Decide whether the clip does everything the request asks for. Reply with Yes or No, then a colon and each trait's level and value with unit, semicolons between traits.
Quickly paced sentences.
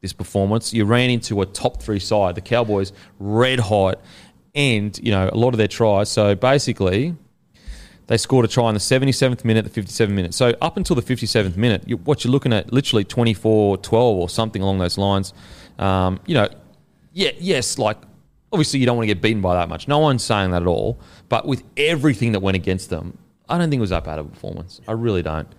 Yes: fast, 225 wpm